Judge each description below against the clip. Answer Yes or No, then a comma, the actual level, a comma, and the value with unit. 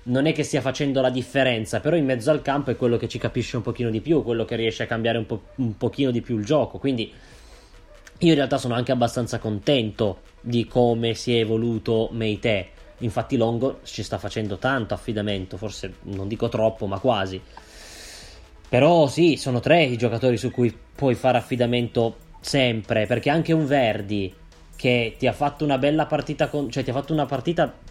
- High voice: No, low, 120 Hz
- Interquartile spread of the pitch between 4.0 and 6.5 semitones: No, average, 3.4 semitones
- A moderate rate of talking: No, fast, 195 wpm